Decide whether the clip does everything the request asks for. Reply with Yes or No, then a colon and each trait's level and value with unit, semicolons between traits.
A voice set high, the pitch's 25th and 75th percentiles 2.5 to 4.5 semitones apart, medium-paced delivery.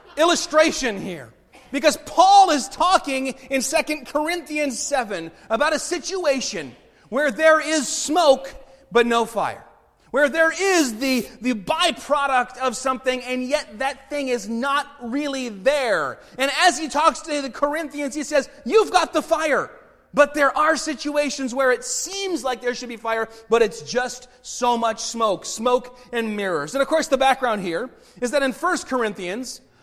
Yes: very high, 270 Hz; average, 3.7 semitones; average, 165 wpm